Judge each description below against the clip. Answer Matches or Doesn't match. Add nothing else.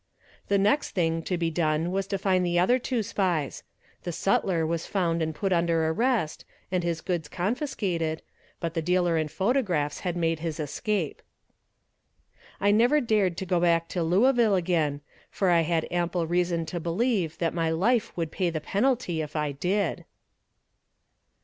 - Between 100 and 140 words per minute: Doesn't match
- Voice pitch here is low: Doesn't match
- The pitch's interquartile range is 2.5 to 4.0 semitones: Matches